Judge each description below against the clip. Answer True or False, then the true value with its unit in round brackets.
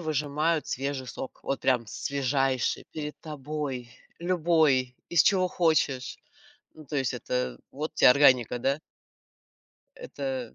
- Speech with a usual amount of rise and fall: True (3.2 semitones)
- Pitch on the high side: False (140 Hz)